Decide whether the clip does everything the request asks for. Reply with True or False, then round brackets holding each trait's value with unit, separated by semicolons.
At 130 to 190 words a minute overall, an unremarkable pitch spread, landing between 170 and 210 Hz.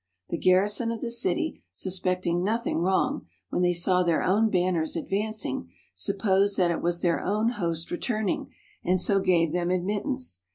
True (160 wpm; 3.4 semitones; 185 Hz)